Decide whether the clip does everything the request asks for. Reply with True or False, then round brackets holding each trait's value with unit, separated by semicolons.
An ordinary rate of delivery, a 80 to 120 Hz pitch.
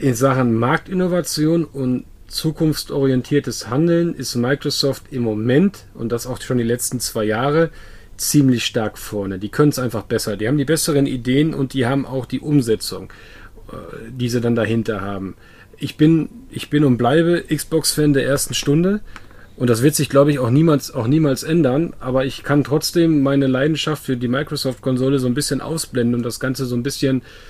False (180 wpm; 135 Hz)